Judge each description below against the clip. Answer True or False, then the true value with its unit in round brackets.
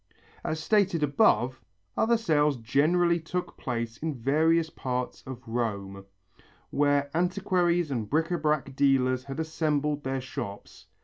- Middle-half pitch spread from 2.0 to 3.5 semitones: False (4.4 semitones)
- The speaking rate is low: True (130 wpm)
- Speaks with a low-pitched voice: False (145 Hz)